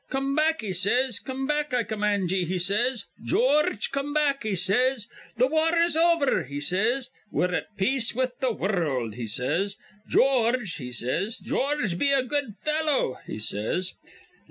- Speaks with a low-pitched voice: No, high, 235 Hz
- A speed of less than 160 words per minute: No, average, 165 wpm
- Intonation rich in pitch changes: Yes, wide, 6.9 semitones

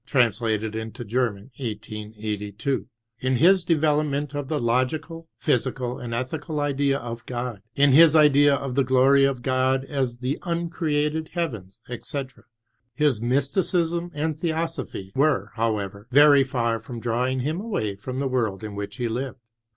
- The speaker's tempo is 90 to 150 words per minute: Yes, average, 145 wpm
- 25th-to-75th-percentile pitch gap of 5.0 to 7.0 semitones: No, average, 4.2 semitones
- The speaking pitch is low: Yes, low, 130 Hz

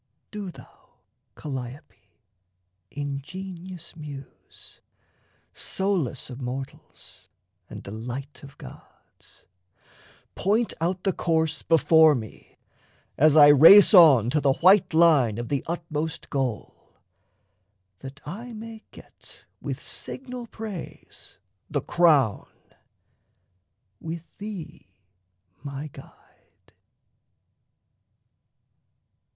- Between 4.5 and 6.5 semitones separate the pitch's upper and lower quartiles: Yes, average, 5.1 semitones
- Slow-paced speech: Yes, slow, 90 wpm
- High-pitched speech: No, medium, 155 Hz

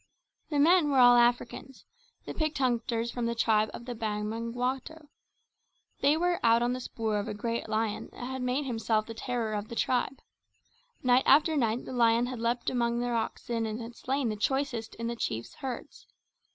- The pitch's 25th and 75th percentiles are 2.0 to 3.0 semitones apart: Yes, narrow, 2.4 semitones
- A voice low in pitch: No, high, 240 Hz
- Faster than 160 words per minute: Yes, average, 190 wpm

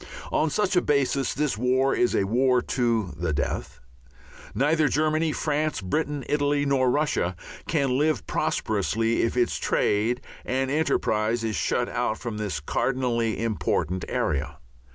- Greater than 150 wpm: No, average, 140 wpm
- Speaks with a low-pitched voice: Yes, low, 125 Hz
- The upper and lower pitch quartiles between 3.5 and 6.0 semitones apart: Yes, average, 5.2 semitones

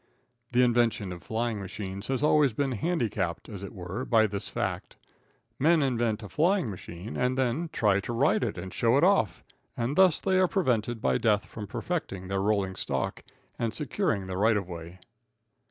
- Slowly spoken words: No, average, 185 wpm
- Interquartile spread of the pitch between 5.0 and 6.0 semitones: Yes, average, 5.3 semitones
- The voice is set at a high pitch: No, low, 115 Hz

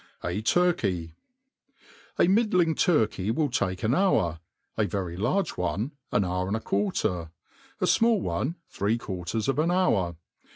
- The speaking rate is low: No, average, 150 wpm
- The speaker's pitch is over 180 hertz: No, low, 110 Hz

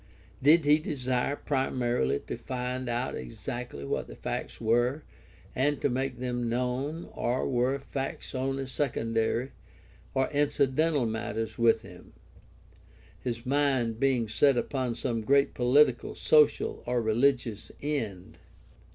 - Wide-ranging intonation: No, average, 2.9 semitones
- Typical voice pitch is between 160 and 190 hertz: No, low, 125 Hz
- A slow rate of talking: Yes, slow, 125 wpm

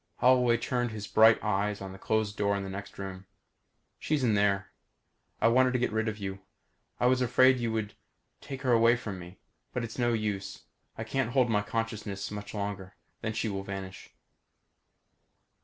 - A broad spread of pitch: No, average, 3.2 semitones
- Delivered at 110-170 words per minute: No, average, 185 wpm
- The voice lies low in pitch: Yes, low, 110 Hz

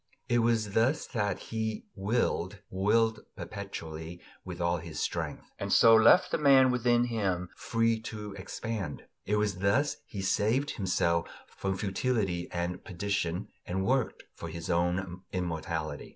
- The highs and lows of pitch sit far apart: No, average, 4.4 semitones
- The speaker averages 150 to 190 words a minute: No, average, 140 wpm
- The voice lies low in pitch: Yes, low, 100 Hz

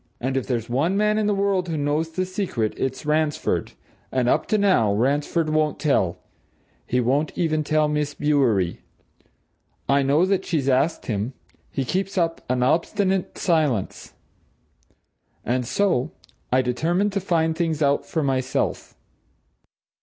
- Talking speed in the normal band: Yes, average, 145 wpm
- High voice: No, medium, 150 Hz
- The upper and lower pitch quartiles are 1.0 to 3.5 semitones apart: No, average, 5.1 semitones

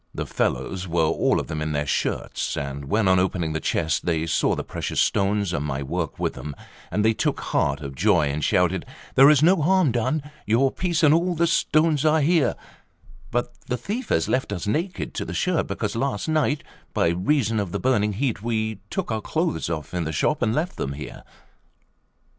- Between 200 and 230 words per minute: Yes, fast, 205 wpm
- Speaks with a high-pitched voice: No, low, 110 Hz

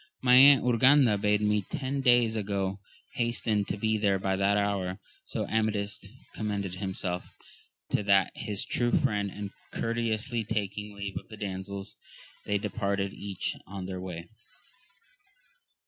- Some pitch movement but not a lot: No, narrow, 2.2 semitones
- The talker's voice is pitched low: Yes, low, 105 Hz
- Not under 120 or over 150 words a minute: Yes, average, 145 wpm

